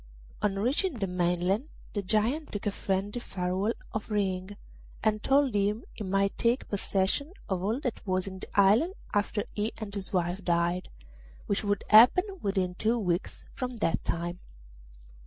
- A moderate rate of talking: Yes, average, 160 wpm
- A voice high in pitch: Yes, high, 200 Hz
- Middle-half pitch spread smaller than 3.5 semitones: Yes, average, 3.0 semitones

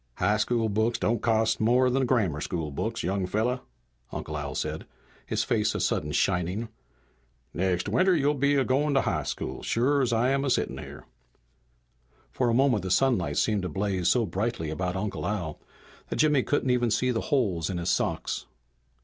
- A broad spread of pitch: Yes, wide, 5.7 semitones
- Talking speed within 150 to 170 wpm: No, average, 185 wpm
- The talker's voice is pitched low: Yes, low, 110 Hz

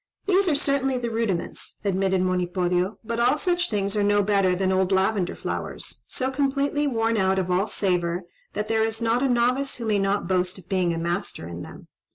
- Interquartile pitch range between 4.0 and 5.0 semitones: Yes, average, 4.5 semitones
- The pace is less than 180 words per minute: No, fast, 205 wpm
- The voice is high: Yes, high, 205 Hz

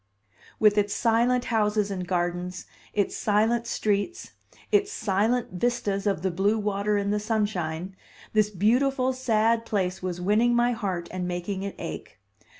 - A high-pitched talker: Yes, high, 210 Hz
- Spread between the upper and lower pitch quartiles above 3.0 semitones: Yes, average, 3.4 semitones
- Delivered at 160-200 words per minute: No, average, 150 wpm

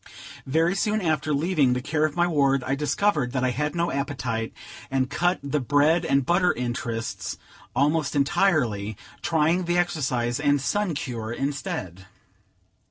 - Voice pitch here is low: No, medium, 145 Hz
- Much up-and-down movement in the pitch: No, average, 4.5 semitones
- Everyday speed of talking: Yes, average, 150 wpm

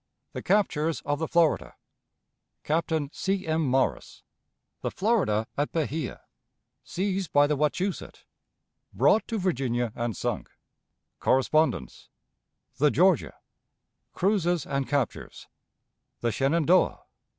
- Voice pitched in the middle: Yes, medium, 155 Hz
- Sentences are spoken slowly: Yes, slow, 105 wpm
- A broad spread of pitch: No, average, 4.9 semitones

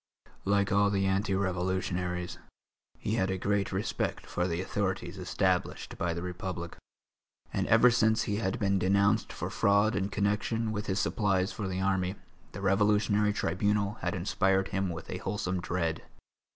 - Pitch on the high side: No, very low, 95 Hz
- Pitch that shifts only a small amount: Yes, narrow, 1.8 semitones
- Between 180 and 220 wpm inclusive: No, average, 160 wpm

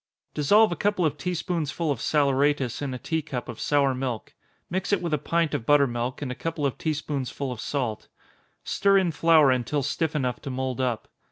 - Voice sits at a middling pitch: Yes, medium, 145 Hz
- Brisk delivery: Yes, fast, 215 wpm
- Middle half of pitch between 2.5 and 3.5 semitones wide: No, average, 4.0 semitones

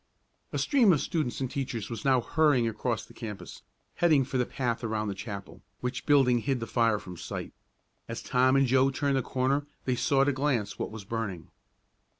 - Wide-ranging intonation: No, average, 3.3 semitones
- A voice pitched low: Yes, low, 125 Hz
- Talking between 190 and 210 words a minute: Yes, average, 200 wpm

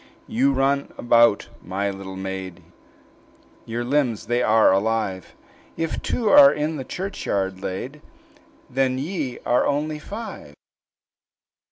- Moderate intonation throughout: No, wide, 7.1 semitones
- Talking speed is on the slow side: Yes, slow, 120 wpm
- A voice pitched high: No, low, 120 Hz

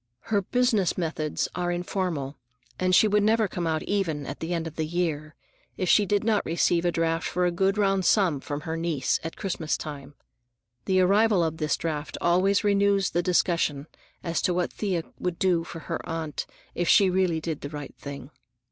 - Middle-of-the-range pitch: Yes, medium, 175 Hz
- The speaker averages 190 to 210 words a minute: Yes, average, 195 wpm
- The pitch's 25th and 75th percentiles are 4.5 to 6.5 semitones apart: No, average, 3.3 semitones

